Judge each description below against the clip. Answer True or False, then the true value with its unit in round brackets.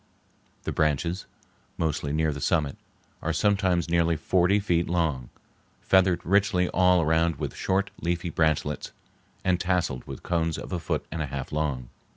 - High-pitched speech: False (85 Hz)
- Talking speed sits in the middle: True (150 wpm)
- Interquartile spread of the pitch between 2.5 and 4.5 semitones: True (2.9 semitones)